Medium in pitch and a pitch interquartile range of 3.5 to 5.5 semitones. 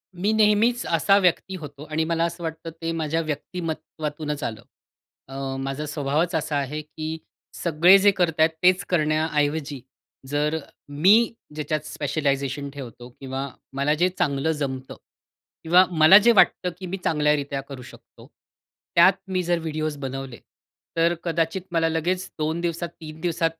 No: medium, 155 Hz; average, 3.0 semitones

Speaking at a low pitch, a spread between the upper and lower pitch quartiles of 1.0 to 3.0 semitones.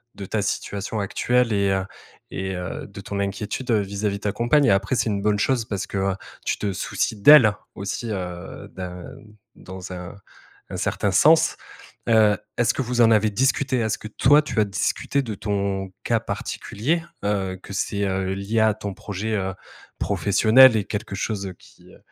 Yes: low, 105 Hz; narrow, 2.5 semitones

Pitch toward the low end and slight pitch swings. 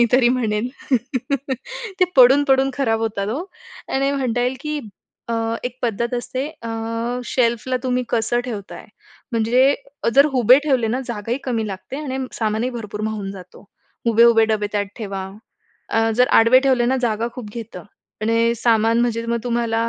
No: high, 235 Hz; narrow, 2.3 semitones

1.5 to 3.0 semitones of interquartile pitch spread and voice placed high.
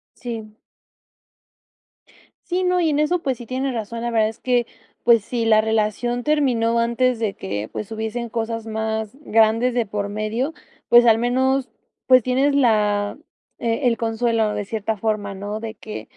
Yes: narrow, 2.4 semitones; high, 230 Hz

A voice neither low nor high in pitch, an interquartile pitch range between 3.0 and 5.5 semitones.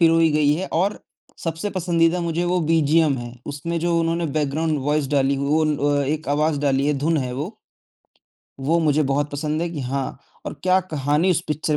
No: medium, 155 Hz; narrow, 2.6 semitones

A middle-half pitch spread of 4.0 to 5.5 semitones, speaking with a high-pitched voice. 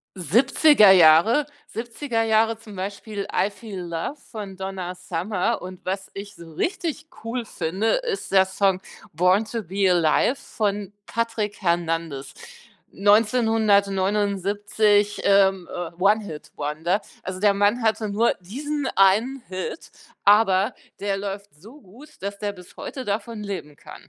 No: average, 3.1 semitones; high, 200 Hz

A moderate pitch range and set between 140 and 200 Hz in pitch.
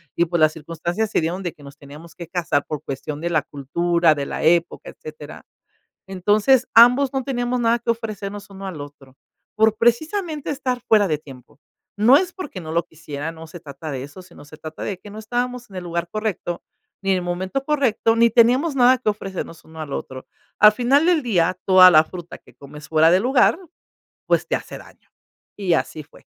No: wide, 6.7 semitones; medium, 185 Hz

